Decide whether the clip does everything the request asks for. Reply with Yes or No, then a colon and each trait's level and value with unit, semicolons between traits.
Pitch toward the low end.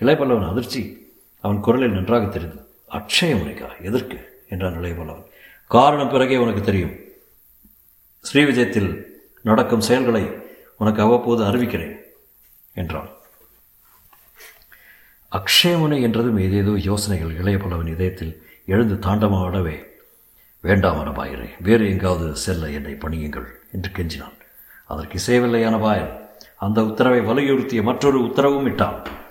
Yes: low, 100 Hz